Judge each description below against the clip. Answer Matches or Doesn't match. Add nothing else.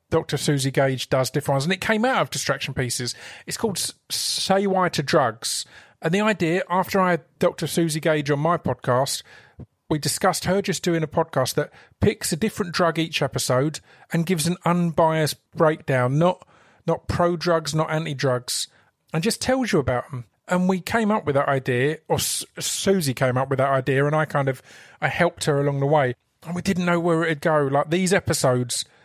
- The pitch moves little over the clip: Doesn't match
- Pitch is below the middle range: Doesn't match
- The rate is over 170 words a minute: Matches